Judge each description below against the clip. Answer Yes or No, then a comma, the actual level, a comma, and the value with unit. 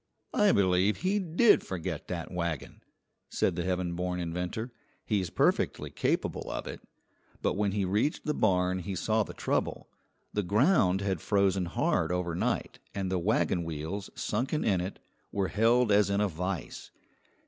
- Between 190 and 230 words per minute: No, average, 160 wpm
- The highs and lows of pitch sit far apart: No, average, 2.9 semitones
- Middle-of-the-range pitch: No, very low, 95 Hz